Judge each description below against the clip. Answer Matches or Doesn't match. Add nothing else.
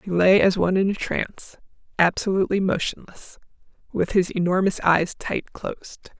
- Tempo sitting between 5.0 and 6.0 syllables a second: Matches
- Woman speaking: Matches